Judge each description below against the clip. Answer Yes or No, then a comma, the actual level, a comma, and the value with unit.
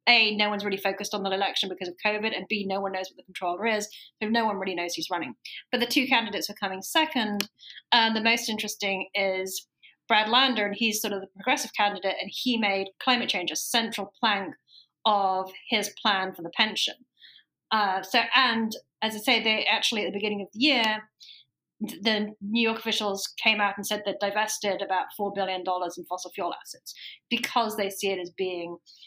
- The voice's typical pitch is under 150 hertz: No, high, 205 Hz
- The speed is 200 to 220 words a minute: Yes, fast, 205 wpm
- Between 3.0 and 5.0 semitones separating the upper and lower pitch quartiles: No, narrow, 2.6 semitones